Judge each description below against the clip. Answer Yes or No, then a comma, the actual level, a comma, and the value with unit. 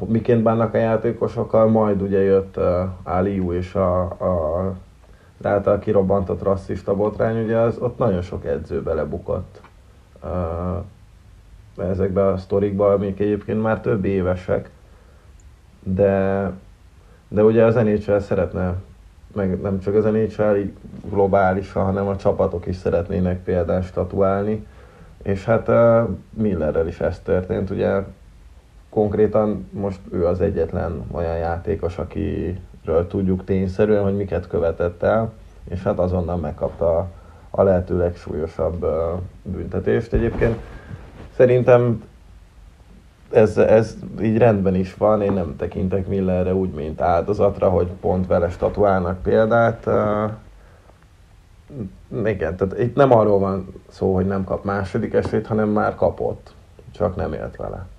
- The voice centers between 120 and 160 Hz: No, very low, 95 Hz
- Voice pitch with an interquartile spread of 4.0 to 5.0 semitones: No, narrow, 2.5 semitones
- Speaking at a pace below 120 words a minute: No, average, 125 wpm